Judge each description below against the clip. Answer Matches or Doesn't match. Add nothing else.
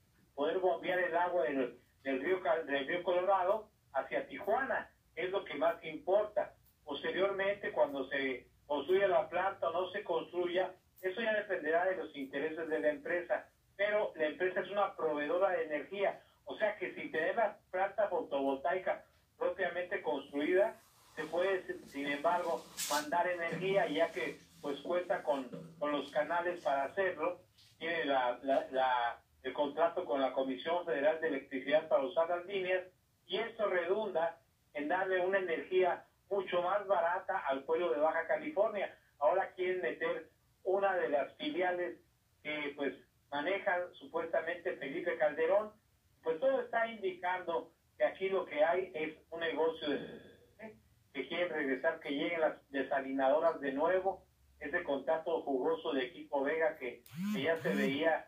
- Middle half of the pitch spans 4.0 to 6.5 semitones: Matches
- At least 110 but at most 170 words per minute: Matches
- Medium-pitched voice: Matches